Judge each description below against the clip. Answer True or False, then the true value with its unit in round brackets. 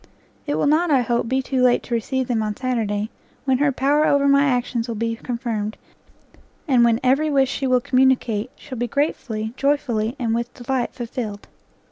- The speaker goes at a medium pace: True (185 wpm)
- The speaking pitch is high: True (250 Hz)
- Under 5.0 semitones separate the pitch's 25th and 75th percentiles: True (2.8 semitones)